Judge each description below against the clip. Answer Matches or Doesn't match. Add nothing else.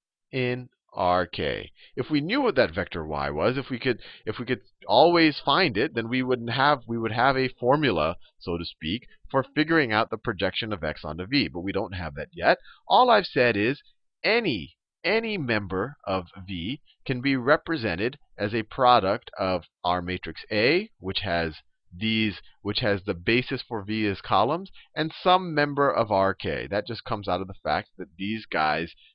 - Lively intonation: Matches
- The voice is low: Matches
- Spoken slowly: Doesn't match